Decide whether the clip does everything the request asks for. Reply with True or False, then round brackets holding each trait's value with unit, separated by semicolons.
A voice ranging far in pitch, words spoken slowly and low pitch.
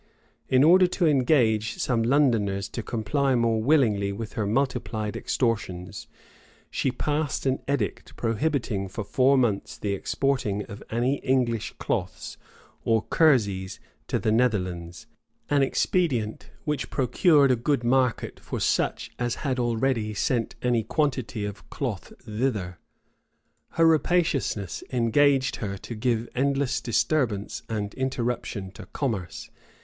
False (4.4 semitones; 125 wpm; 120 Hz)